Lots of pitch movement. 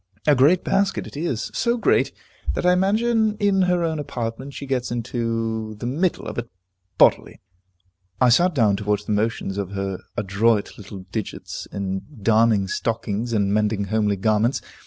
Yes: wide, 6.5 semitones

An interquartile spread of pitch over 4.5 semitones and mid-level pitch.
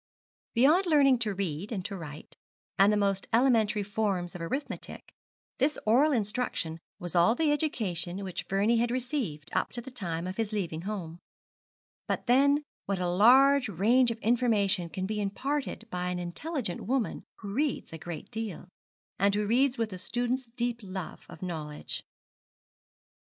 No: wide, 5.5 semitones; high, 210 Hz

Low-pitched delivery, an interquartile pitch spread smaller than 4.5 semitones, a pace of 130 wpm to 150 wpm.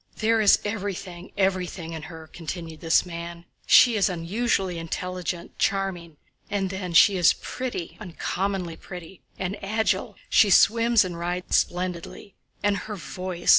No: medium, 185 Hz; average, 2.8 semitones; slow, 135 wpm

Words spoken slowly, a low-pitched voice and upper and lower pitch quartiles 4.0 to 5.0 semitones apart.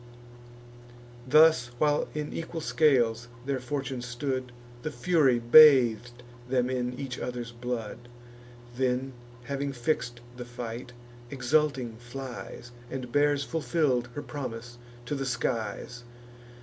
No: slow, 110 wpm; low, 125 Hz; average, 2.8 semitones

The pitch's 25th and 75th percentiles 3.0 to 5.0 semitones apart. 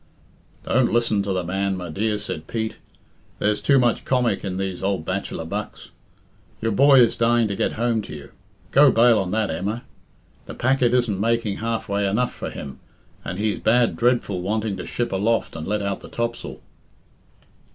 Yes: average, 3.3 semitones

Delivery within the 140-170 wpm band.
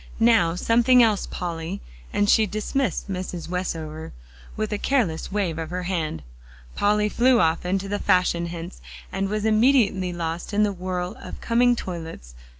Yes: average, 155 wpm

